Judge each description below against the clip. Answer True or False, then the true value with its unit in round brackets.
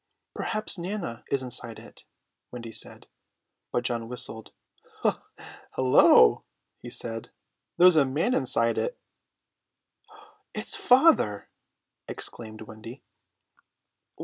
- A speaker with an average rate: False (95 wpm)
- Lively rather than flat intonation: True (7.6 semitones)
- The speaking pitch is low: True (125 Hz)